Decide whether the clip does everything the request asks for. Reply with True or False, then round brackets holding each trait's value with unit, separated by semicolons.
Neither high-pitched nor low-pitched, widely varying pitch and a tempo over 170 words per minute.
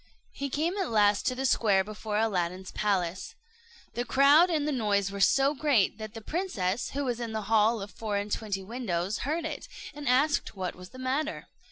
False (225 Hz; 5.7 semitones; 200 wpm)